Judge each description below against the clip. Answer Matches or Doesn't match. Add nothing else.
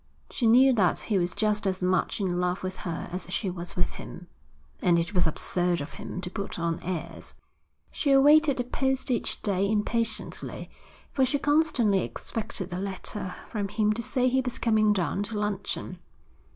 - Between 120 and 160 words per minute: Doesn't match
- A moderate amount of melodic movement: Matches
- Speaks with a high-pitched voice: Matches